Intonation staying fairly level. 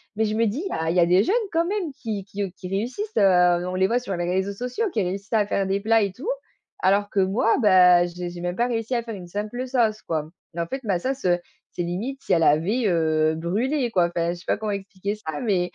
No: average, 4.5 semitones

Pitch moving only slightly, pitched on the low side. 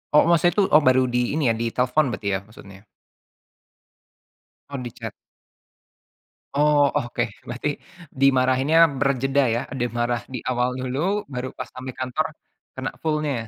No: average, 3.2 semitones; low, 130 Hz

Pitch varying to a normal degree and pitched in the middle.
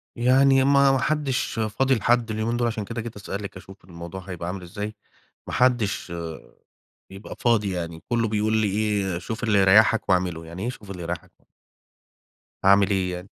No: average, 3.9 semitones; low, 105 Hz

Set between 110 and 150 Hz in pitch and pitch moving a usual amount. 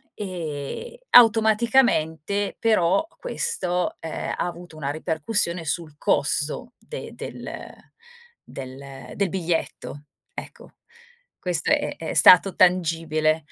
No: medium, 170 Hz; average, 4.7 semitones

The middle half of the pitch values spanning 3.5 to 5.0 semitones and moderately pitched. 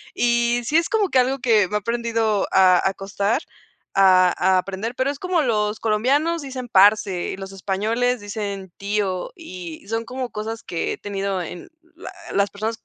No: average, 4.1 semitones; high, 215 Hz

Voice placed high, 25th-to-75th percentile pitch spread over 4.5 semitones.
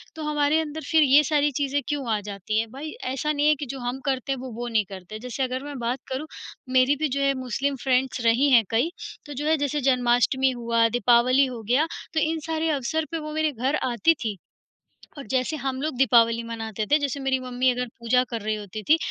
No: very high, 260 Hz; average, 3.3 semitones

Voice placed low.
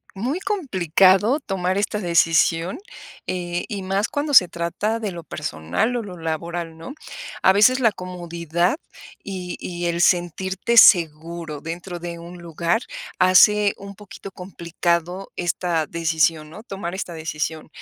No: medium, 175 Hz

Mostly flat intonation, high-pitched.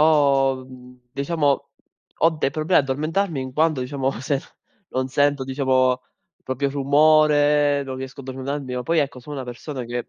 No: narrow, 2.1 semitones; medium, 140 Hz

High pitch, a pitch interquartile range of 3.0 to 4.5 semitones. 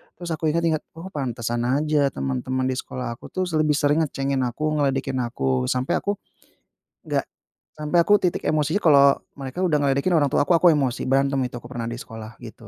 No: medium, 140 Hz; average, 3.4 semitones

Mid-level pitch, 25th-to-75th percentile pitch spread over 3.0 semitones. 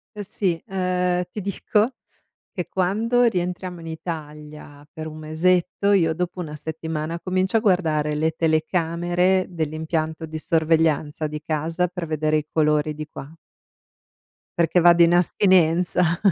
No: medium, 165 Hz; narrow, 2.5 semitones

